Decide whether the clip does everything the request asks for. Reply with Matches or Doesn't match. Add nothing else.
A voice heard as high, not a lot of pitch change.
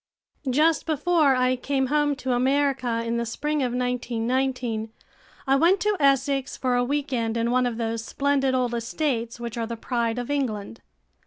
Doesn't match